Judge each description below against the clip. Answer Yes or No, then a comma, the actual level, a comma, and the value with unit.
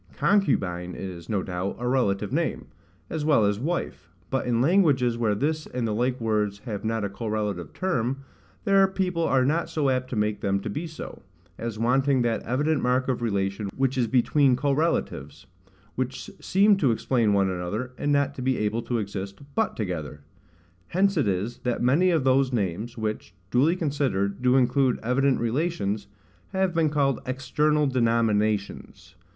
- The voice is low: Yes, low, 125 Hz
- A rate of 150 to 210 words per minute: Yes, average, 170 wpm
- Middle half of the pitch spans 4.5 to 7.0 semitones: Yes, average, 5.2 semitones